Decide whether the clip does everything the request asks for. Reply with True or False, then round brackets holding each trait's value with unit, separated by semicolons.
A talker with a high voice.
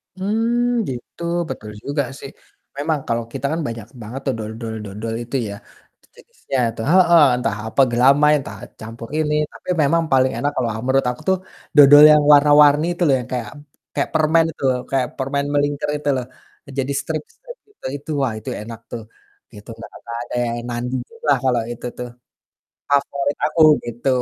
False (135 Hz)